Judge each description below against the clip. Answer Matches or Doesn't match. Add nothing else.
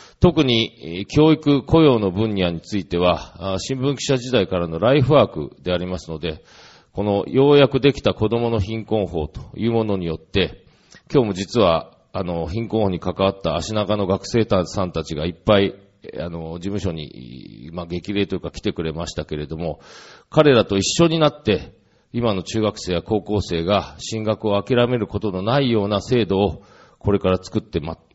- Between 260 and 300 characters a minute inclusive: Doesn't match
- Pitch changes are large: Doesn't match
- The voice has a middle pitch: Doesn't match